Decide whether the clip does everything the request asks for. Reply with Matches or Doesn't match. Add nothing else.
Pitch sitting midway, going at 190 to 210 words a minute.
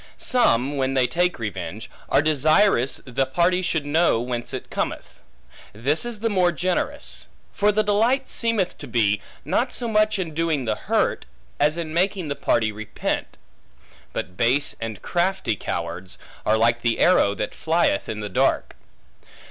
Doesn't match